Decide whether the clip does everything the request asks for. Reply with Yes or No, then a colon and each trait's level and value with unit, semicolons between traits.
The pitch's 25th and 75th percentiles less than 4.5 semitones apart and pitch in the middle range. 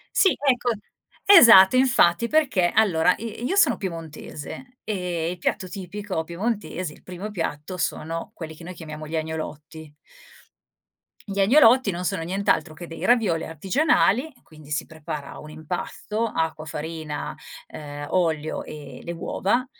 No: average, 5.2 semitones; medium, 175 Hz